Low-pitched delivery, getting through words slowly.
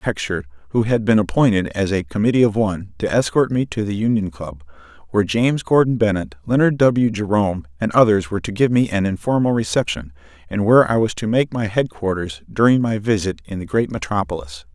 No: low, 105 Hz; average, 195 wpm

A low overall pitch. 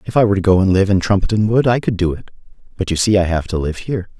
Yes: low, 100 Hz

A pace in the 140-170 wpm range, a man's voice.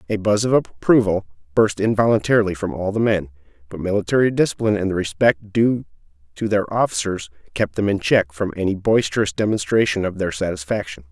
Yes: average, 165 wpm; male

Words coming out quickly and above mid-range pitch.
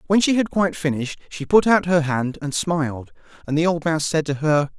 No: fast, 240 wpm; medium, 160 Hz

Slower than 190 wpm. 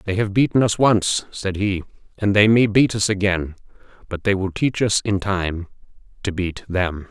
No: average, 195 wpm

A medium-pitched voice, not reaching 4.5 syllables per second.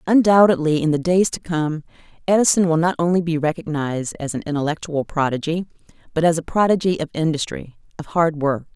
No: medium, 165 Hz; 5.8 syllables/s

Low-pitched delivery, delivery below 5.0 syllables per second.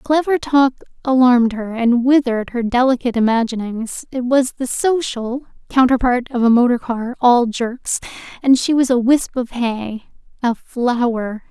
No: high, 245 Hz; 4.5 syllables/s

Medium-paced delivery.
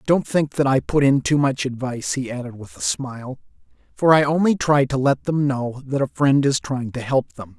No: fast, 235 wpm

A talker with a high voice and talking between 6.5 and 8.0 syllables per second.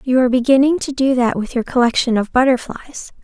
Yes: very high, 255 Hz; 6.7 syllables/s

